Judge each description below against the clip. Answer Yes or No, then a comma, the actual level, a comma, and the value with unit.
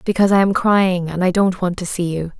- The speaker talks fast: Yes, fast, 275 wpm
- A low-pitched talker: No, medium, 185 Hz